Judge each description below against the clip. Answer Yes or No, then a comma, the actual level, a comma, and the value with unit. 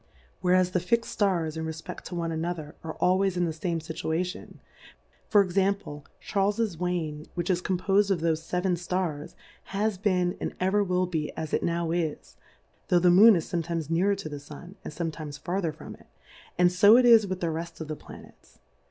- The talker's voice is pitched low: No, medium, 175 Hz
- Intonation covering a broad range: No, average, 2.8 semitones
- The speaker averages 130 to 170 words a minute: No, average, 190 wpm